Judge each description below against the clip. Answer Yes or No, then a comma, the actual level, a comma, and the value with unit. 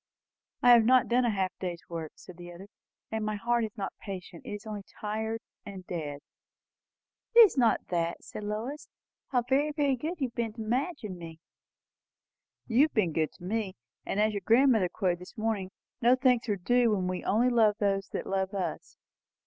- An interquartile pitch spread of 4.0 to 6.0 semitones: Yes, average, 4.5 semitones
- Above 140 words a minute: Yes, average, 200 wpm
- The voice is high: Yes, high, 215 Hz